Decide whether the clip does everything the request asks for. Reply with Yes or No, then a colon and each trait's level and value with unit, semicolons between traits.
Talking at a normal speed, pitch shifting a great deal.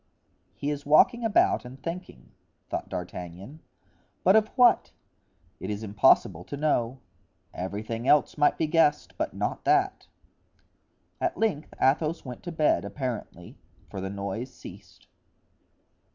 No: slow, 130 wpm; wide, 8.4 semitones